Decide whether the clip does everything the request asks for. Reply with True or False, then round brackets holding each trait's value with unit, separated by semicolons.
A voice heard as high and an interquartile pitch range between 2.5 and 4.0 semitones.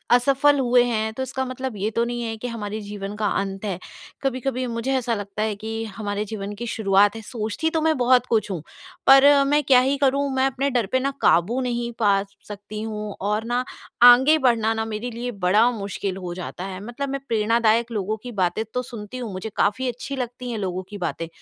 True (230 Hz; 3.6 semitones)